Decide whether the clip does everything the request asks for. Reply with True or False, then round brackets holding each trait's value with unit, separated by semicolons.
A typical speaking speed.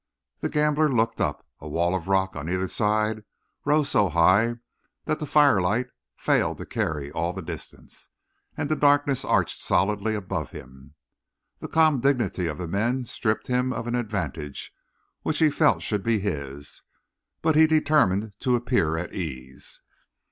True (160 wpm)